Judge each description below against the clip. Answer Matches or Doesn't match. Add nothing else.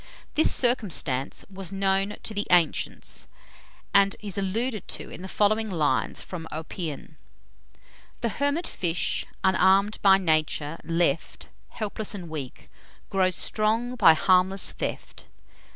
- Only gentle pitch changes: Doesn't match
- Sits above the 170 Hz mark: Matches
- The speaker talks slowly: Matches